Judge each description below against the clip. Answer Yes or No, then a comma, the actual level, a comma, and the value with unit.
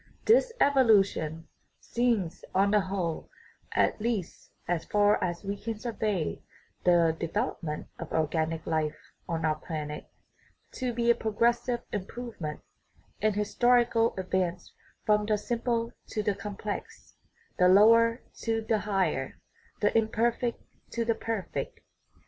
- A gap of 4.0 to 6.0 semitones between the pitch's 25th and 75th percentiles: Yes, average, 4.9 semitones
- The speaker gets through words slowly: Yes, slow, 125 wpm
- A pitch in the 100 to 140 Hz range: No, high, 210 Hz